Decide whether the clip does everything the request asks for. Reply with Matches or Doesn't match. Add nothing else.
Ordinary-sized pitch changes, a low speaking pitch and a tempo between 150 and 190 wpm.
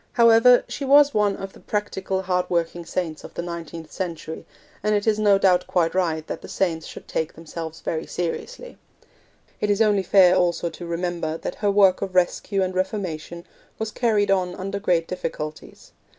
Doesn't match